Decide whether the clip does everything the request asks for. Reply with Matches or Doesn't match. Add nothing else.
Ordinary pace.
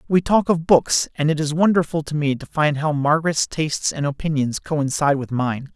Doesn't match